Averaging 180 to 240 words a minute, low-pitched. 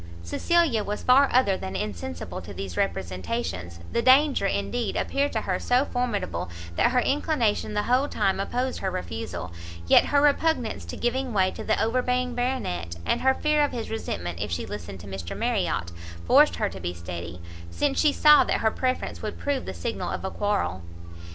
No: average, 185 wpm; high, 215 Hz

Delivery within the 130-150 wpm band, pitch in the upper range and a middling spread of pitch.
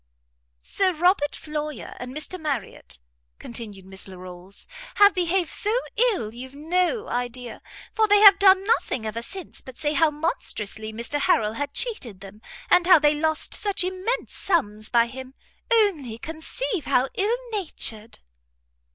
No: average, 145 wpm; very high, 300 Hz; wide, 8.3 semitones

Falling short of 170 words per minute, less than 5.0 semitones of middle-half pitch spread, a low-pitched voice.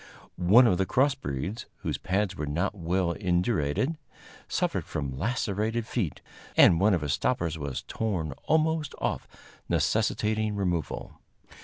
No: slow, 135 wpm; wide, 5.5 semitones; very low, 95 Hz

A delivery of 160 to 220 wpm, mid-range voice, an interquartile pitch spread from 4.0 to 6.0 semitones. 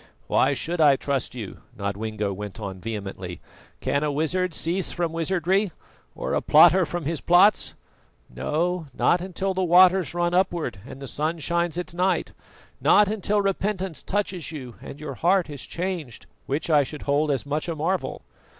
Yes: average, 170 wpm; medium, 165 Hz; average, 4.6 semitones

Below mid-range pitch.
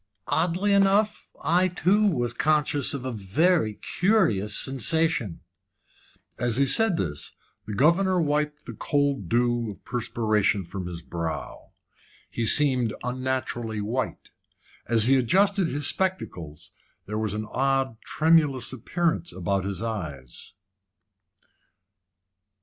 Yes: low, 130 Hz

